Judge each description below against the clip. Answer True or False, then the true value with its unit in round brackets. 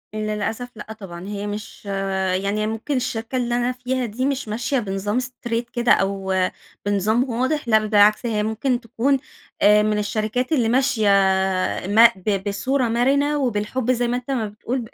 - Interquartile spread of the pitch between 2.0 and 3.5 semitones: True (3.1 semitones)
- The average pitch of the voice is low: False (230 Hz)